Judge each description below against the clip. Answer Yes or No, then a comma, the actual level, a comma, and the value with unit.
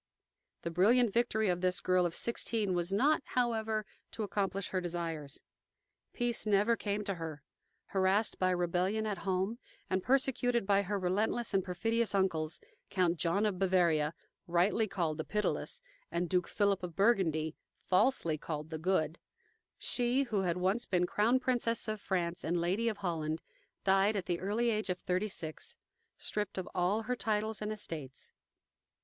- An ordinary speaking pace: Yes, average, 160 wpm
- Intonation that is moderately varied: Yes, average, 3.8 semitones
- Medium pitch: No, high, 195 Hz